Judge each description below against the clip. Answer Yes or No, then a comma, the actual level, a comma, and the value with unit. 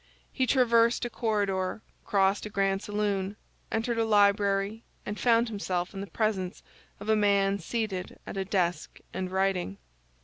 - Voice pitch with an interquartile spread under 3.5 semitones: Yes, narrow, 2.4 semitones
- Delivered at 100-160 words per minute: Yes, average, 150 wpm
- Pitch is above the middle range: Yes, high, 200 Hz